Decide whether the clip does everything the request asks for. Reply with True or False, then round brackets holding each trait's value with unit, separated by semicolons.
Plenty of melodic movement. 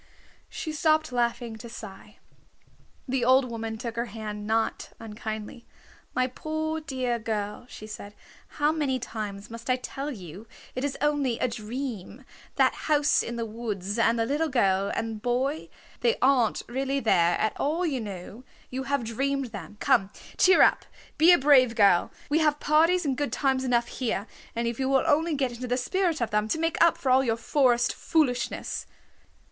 False (4.3 semitones)